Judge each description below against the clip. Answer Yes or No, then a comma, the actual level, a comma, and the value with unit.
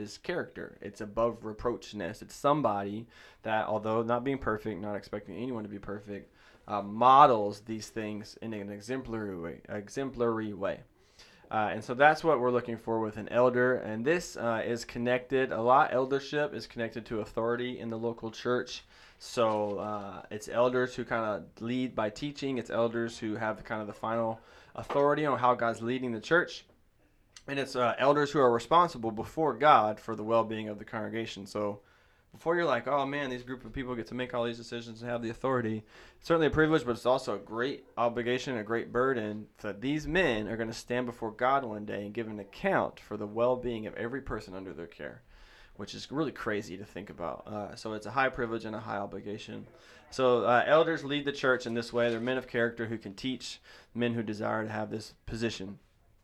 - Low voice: Yes, low, 115 Hz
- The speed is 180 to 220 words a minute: Yes, fast, 205 wpm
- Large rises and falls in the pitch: No, average, 2.8 semitones